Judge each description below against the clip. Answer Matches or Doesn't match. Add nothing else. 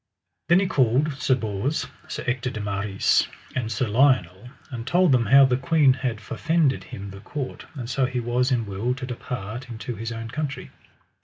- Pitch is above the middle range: Doesn't match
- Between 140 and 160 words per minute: Doesn't match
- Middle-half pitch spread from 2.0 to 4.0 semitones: Matches